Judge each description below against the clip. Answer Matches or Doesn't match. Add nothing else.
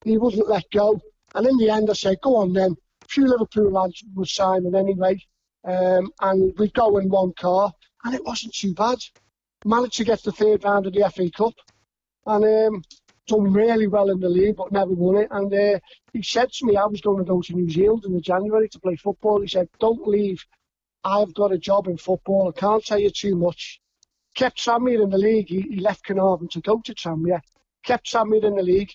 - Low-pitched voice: Doesn't match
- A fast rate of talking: Matches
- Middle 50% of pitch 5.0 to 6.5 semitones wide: Doesn't match